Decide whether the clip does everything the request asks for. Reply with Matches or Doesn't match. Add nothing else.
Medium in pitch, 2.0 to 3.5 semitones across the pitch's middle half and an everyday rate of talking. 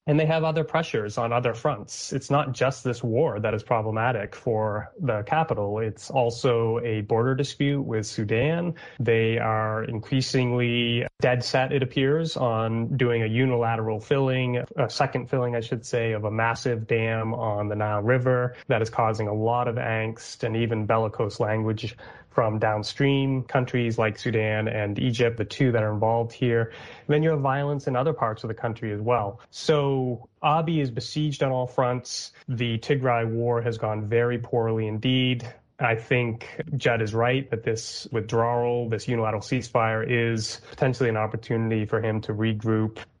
Doesn't match